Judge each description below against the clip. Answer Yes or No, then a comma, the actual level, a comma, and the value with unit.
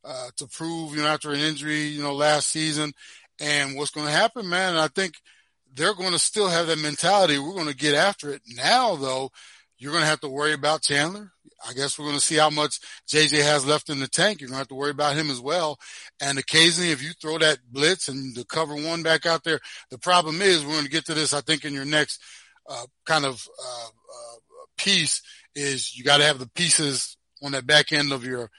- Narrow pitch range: Yes, narrow, 2.2 semitones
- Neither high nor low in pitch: Yes, medium, 150 Hz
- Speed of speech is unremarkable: No, fast, 240 wpm